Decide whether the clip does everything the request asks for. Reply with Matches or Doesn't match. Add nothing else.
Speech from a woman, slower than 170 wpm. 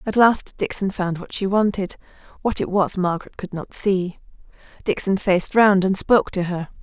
Doesn't match